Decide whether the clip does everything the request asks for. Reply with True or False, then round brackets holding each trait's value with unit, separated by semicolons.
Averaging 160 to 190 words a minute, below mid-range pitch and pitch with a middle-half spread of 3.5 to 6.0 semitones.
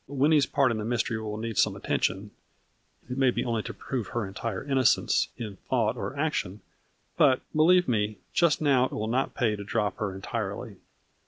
True (185 wpm; 120 Hz; 4.2 semitones)